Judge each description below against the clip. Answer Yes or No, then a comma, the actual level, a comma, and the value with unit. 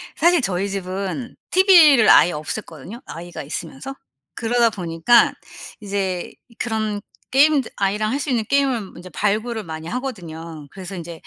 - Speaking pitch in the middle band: No, high, 205 Hz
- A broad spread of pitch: Yes, wide, 5.8 semitones